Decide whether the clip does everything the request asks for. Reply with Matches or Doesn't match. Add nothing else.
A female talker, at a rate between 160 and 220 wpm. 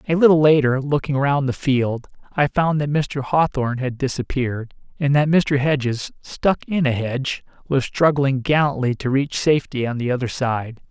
Doesn't match